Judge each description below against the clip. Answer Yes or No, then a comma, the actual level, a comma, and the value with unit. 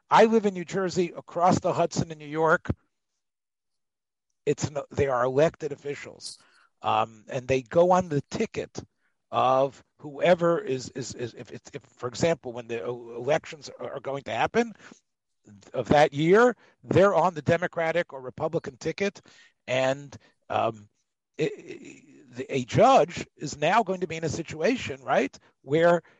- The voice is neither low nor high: Yes, medium, 150 Hz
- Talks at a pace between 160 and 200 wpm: No, average, 150 wpm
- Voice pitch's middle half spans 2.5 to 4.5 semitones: No, average, 5.2 semitones